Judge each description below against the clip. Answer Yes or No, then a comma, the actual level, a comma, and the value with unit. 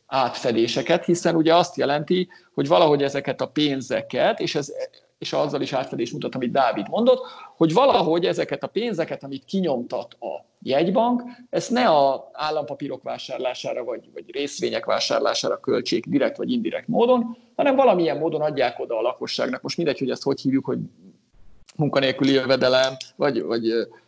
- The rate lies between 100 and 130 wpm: No, average, 150 wpm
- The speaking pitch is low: No, medium, 150 Hz